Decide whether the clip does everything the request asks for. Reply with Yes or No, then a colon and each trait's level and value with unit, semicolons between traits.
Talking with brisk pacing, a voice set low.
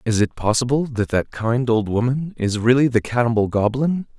No: average, 185 wpm; low, 120 Hz